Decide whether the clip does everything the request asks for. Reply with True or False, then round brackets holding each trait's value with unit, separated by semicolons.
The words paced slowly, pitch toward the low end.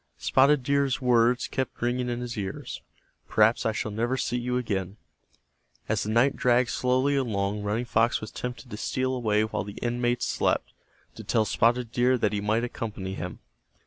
False (175 wpm; 120 Hz)